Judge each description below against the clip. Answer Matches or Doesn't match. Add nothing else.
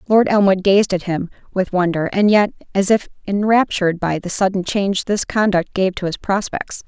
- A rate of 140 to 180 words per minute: Doesn't match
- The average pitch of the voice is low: Doesn't match